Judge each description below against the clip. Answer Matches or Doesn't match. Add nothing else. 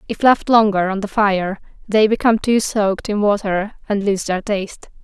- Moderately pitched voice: Doesn't match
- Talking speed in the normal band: Matches